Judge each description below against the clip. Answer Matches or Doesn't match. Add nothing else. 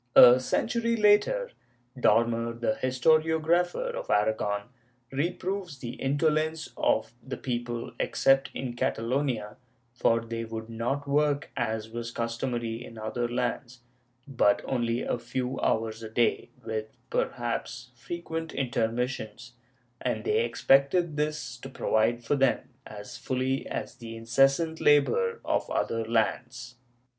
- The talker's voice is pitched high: Doesn't match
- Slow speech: Matches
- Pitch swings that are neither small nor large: Matches